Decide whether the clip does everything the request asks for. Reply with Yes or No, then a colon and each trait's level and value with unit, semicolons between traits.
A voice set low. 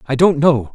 No: medium, 145 Hz